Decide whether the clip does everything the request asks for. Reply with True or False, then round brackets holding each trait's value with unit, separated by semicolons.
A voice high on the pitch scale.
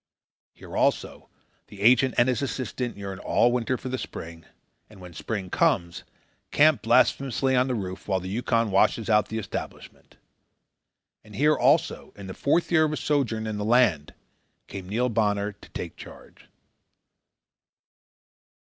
False (110 Hz)